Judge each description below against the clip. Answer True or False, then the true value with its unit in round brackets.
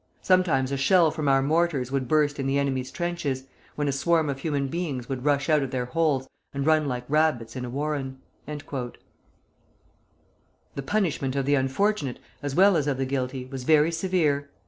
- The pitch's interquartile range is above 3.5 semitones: False (3.0 semitones)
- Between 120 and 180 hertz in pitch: True (140 Hz)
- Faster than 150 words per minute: True (185 wpm)